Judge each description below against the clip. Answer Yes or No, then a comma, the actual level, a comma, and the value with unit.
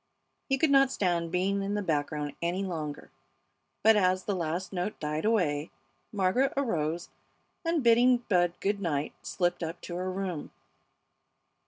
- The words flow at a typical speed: Yes, average, 150 wpm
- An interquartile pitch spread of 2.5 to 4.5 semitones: Yes, average, 4.0 semitones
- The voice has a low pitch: No, medium, 185 Hz